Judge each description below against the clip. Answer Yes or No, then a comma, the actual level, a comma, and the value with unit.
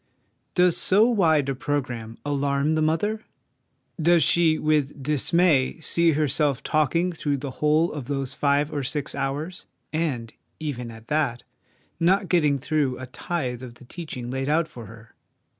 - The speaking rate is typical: Yes, average, 160 wpm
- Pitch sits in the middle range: Yes, medium, 145 Hz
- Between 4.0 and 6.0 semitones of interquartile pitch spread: No, average, 3.6 semitones